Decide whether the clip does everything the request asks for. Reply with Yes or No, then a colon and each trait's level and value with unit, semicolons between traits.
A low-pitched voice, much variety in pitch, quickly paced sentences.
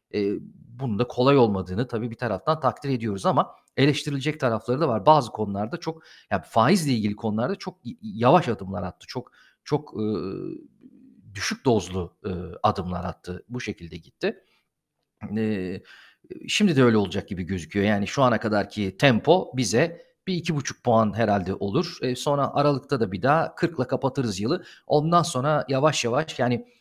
Yes: low, 125 Hz; wide, 6.3 semitones; fast, 155 wpm